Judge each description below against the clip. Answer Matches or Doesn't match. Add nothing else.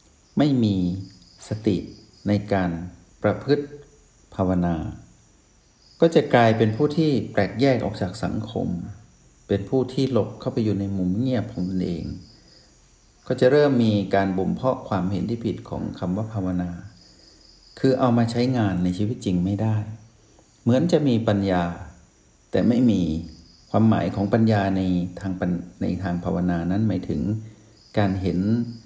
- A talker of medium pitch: Doesn't match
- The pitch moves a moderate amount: Matches